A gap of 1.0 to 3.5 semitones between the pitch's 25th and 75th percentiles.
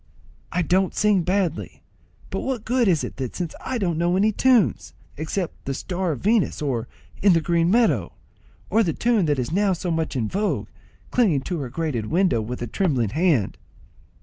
No: wide, 5.4 semitones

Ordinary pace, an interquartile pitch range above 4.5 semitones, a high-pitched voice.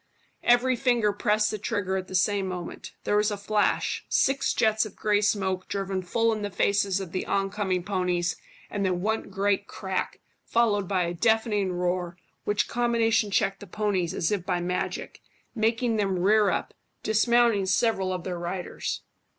No: average, 175 wpm; average, 2.7 semitones; high, 200 Hz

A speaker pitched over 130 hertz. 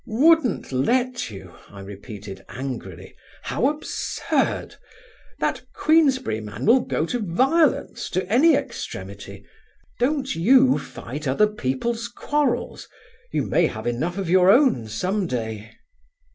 Yes: medium, 185 Hz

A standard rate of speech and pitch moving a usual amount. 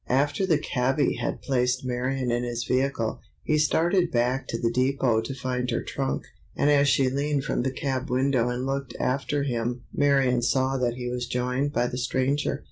No: average, 190 wpm; narrow, 2.0 semitones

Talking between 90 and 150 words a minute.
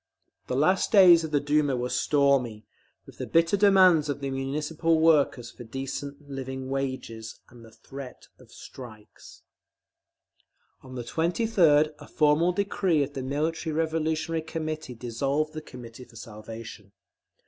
Yes: average, 140 wpm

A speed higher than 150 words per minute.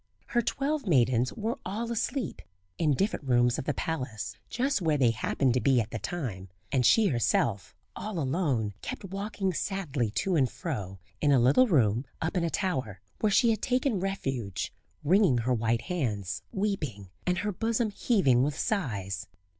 Yes: average, 170 wpm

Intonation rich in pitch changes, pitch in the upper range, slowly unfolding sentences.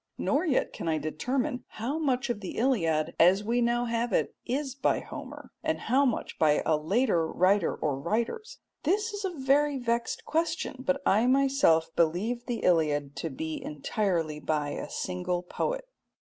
No: wide, 8.7 semitones; high, 235 Hz; average, 170 wpm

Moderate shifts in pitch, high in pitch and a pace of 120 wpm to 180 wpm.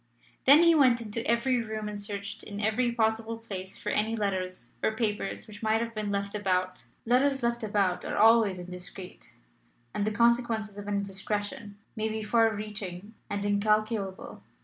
No: narrow, 2.2 semitones; high, 215 Hz; average, 170 wpm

